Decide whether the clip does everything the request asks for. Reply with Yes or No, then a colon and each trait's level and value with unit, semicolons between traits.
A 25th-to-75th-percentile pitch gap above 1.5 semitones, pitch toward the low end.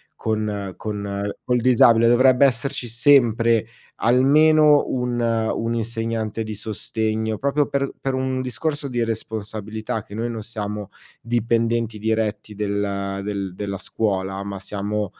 Yes: average, 2.7 semitones; low, 110 Hz